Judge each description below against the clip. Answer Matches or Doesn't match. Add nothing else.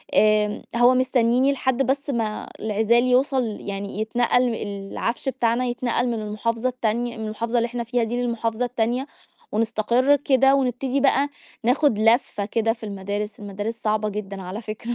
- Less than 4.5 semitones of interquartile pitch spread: Matches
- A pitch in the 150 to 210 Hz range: Doesn't match